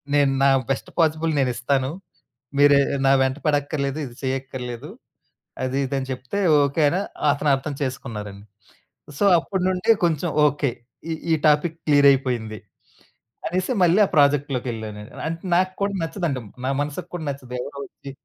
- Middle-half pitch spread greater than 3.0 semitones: Yes, average, 3.4 semitones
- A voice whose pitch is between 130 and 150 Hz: Yes, medium, 140 Hz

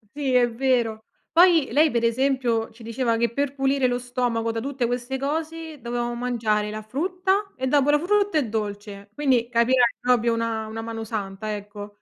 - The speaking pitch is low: No, high, 245 Hz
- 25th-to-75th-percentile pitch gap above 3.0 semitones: Yes, average, 3.5 semitones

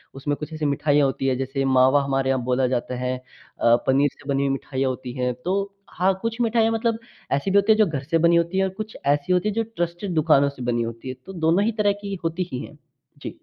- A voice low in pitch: No, medium, 145 Hz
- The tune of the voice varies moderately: No, wide, 6.0 semitones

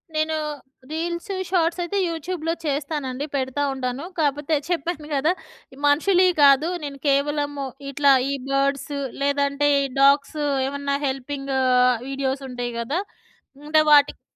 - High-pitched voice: Yes, very high, 285 Hz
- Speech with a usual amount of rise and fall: No, narrow, 2.2 semitones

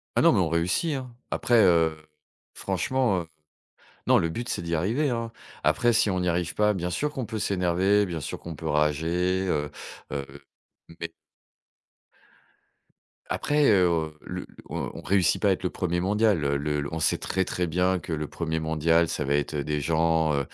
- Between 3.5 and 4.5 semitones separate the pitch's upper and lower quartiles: Yes, average, 4.0 semitones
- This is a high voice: No, very low, 85 Hz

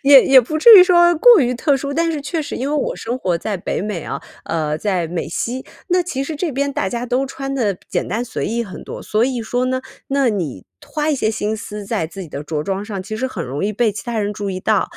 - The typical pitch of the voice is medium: No, high, 235 Hz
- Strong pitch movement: Yes, wide, 5.7 semitones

